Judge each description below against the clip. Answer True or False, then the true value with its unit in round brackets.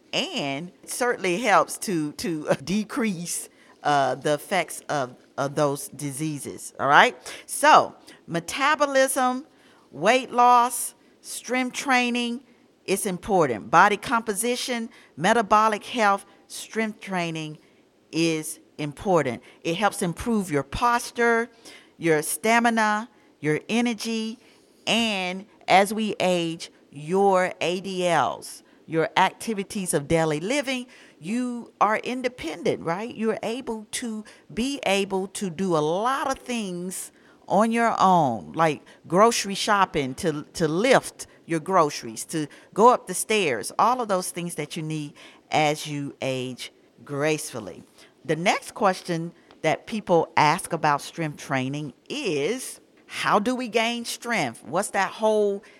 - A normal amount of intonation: False (6.5 semitones)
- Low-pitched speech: False (195 Hz)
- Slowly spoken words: True (120 wpm)